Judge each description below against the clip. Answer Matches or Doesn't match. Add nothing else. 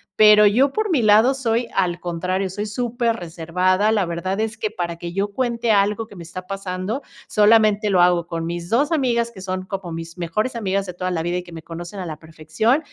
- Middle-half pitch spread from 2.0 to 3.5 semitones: Doesn't match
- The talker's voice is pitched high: Matches